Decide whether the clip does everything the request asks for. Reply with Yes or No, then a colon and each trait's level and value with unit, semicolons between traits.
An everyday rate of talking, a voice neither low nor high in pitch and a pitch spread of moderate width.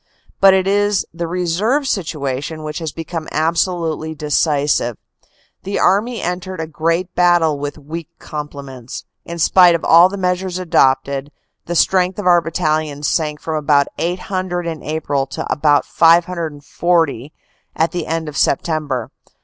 Yes: average, 150 wpm; medium, 165 Hz; average, 3.1 semitones